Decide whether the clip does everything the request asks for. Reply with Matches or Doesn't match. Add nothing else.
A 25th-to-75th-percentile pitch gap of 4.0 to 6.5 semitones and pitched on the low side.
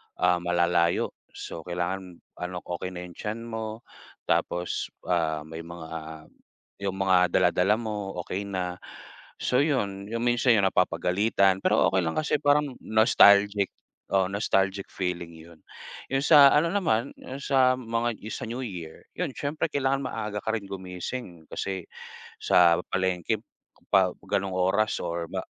Matches